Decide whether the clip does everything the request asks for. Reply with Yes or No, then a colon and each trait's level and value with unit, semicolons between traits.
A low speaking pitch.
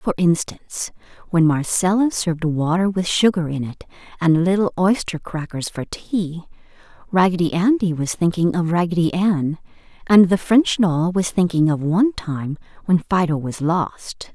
No: medium, 175 Hz